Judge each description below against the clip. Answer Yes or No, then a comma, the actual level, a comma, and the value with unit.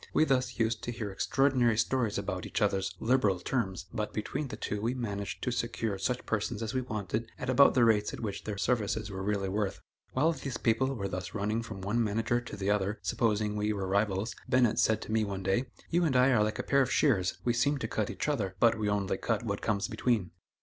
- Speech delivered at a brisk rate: Yes, fast, 235 wpm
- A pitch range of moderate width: Yes, average, 3.5 semitones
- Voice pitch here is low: Yes, low, 110 Hz